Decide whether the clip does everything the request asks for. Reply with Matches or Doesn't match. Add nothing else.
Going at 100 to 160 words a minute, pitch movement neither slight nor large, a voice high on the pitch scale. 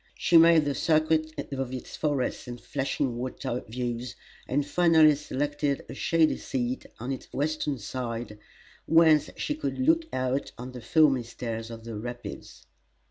Doesn't match